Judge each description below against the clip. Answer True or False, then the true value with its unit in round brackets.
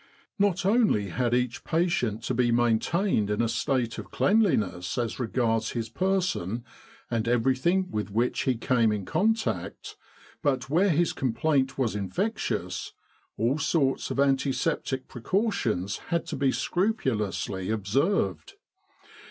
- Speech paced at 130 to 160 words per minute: True (135 wpm)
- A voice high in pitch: False (125 Hz)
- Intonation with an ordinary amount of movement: False (7.2 semitones)